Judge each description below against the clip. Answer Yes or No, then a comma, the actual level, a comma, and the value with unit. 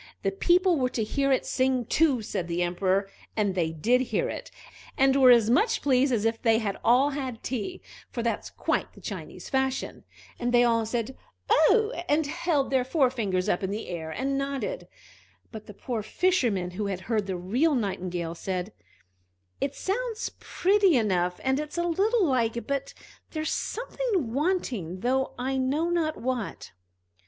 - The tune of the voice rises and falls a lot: Yes, wide, 6.1 semitones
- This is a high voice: Yes, very high, 255 Hz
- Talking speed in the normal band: Yes, average, 170 wpm